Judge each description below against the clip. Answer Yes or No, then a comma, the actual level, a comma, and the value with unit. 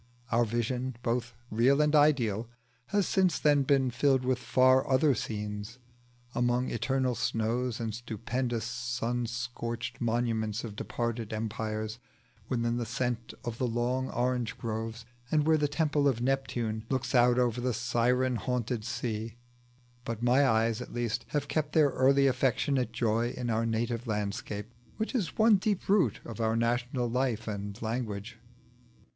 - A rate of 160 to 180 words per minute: No, average, 150 wpm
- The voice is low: Yes, low, 120 Hz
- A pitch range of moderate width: No, narrow, 2.3 semitones